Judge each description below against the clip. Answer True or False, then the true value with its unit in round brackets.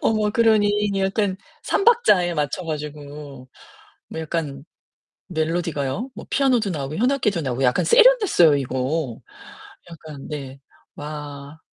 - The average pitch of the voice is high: False (160 Hz)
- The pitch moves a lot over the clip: True (6.5 semitones)